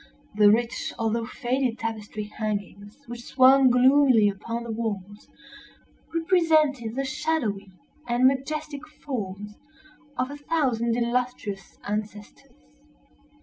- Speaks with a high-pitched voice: Yes, high, 235 Hz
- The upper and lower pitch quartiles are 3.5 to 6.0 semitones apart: Yes, average, 4.2 semitones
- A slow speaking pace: Yes, slow, 105 wpm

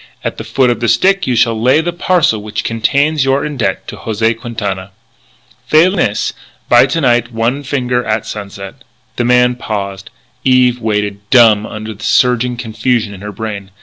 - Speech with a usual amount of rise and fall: Yes, average, 3.0 semitones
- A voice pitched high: No, low, 115 Hz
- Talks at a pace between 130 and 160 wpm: No, average, 175 wpm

